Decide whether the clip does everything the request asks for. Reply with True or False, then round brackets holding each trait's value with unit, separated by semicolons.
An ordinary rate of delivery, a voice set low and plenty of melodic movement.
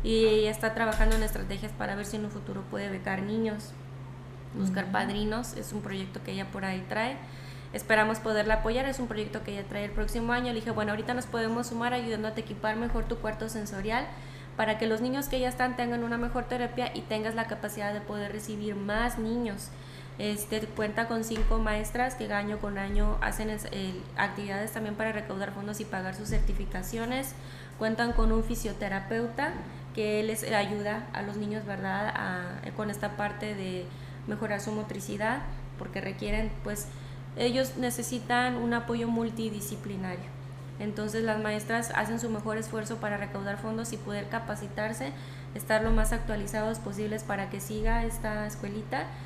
False (170 wpm; 210 Hz; 8.9 semitones)